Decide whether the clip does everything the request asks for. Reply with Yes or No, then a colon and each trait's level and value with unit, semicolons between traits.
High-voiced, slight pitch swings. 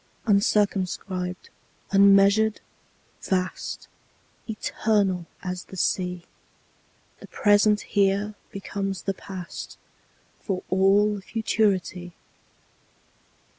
Yes: high, 195 Hz; narrow, 2.0 semitones